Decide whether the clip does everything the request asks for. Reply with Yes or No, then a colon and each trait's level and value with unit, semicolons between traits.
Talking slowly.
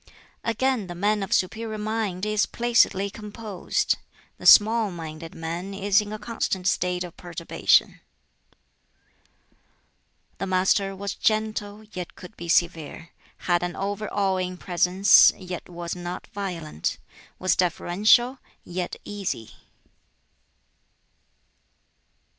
Yes: slow, 110 wpm